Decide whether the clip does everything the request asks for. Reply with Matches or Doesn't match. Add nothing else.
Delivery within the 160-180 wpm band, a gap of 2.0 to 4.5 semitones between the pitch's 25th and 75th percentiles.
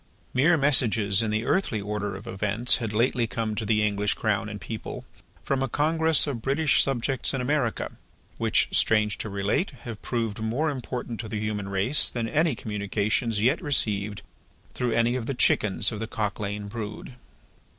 Matches